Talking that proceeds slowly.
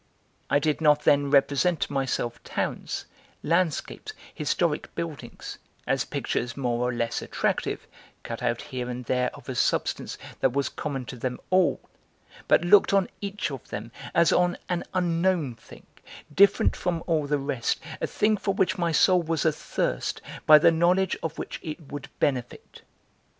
No: average, 160 wpm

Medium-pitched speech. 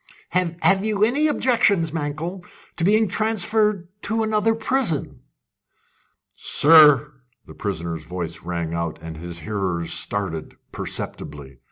Yes: medium, 160 Hz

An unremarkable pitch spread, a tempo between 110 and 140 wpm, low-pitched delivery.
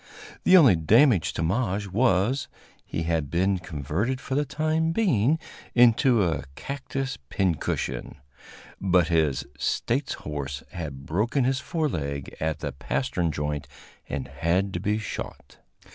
No: wide, 8.7 semitones; slow, 135 wpm; very low, 95 Hz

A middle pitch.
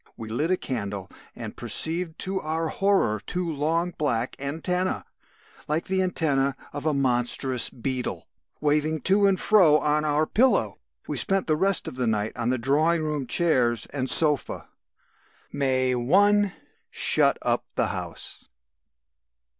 Yes: medium, 150 Hz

